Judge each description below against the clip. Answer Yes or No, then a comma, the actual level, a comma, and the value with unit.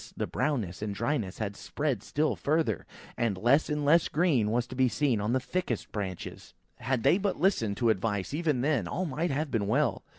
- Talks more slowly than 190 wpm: No, fast, 205 wpm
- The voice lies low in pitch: Yes, low, 125 Hz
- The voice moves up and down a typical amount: No, wide, 6.0 semitones